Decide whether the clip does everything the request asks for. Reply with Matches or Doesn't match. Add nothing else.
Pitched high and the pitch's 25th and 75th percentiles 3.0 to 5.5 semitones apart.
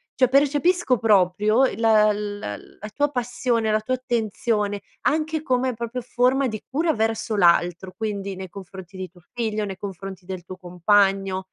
Matches